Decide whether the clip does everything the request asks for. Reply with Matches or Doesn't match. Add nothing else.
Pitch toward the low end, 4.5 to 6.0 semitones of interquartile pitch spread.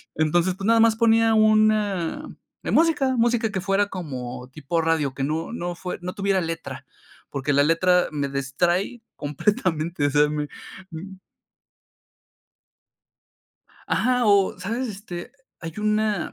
Doesn't match